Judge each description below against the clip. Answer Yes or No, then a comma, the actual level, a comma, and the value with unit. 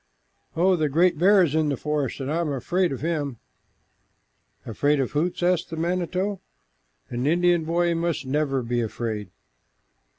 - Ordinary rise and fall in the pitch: Yes, average, 4.2 semitones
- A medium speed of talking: Yes, average, 160 wpm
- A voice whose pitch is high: No, medium, 155 Hz